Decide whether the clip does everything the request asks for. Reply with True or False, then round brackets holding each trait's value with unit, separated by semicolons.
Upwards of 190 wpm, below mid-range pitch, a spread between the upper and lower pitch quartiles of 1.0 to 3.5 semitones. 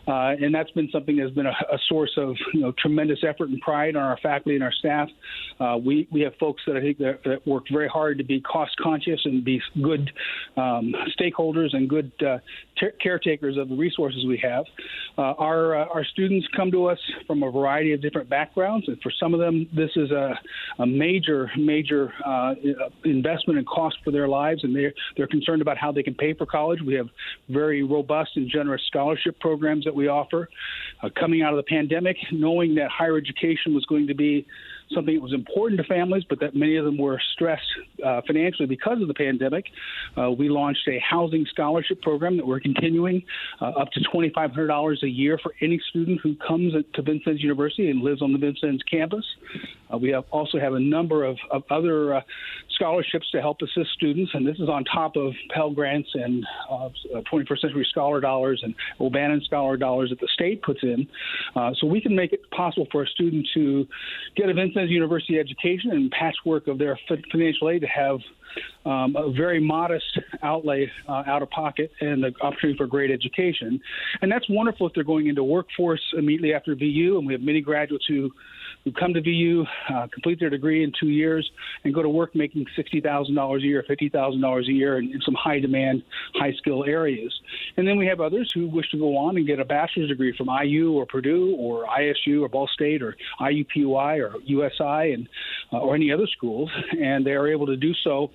False (205 wpm; 150 Hz; 2.8 semitones)